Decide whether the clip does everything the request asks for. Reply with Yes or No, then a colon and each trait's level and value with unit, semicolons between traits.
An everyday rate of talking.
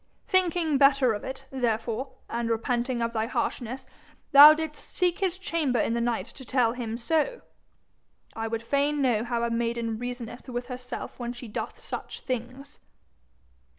Yes: average, 160 wpm